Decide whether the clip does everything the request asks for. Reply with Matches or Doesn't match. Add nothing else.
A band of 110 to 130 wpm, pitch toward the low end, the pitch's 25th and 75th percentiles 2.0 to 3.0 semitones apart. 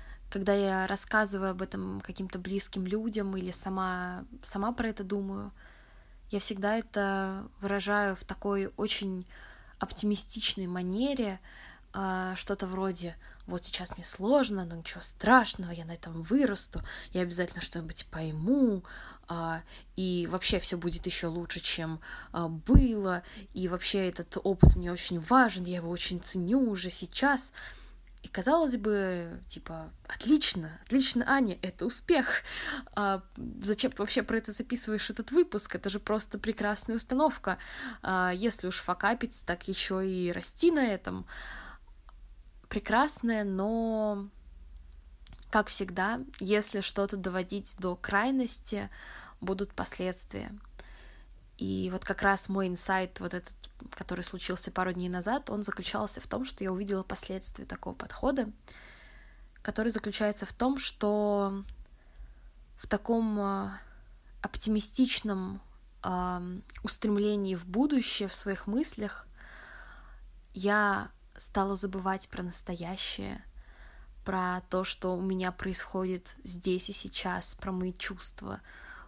Doesn't match